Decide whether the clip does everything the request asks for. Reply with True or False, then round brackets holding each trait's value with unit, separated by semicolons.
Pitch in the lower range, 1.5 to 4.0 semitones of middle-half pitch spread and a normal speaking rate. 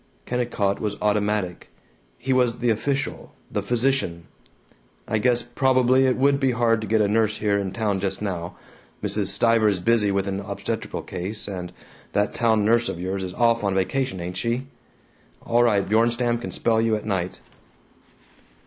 True (110 Hz; 3.3 semitones; 170 wpm)